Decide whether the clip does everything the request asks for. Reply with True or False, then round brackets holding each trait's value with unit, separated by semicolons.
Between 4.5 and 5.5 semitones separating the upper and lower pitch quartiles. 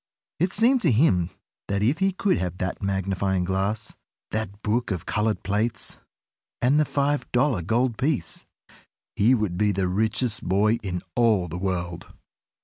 True (4.9 semitones)